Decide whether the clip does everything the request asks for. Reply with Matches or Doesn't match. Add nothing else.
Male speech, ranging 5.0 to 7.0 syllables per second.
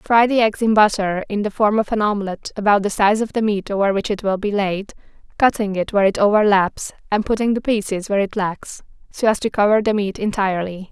Doesn't match